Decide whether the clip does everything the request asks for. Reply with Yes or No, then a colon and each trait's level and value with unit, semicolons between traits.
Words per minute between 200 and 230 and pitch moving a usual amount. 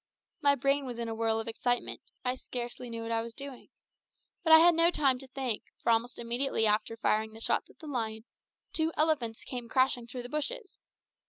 Yes: fast, 205 wpm; average, 3.6 semitones